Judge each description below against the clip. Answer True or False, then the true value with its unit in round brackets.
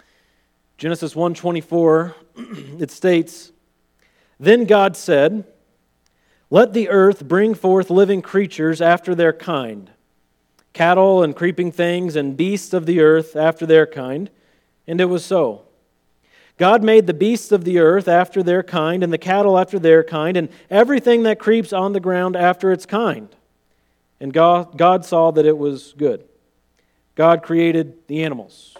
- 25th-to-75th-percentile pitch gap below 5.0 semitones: True (3.4 semitones)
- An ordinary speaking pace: True (150 wpm)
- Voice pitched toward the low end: False (170 Hz)